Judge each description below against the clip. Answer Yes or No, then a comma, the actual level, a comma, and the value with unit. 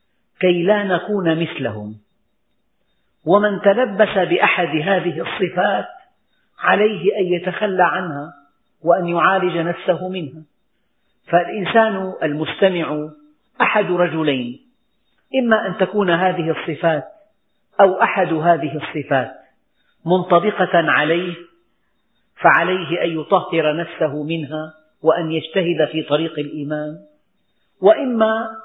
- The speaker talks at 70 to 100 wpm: Yes, average, 90 wpm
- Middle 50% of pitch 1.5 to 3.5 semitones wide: No, average, 4.0 semitones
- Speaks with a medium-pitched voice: Yes, medium, 175 Hz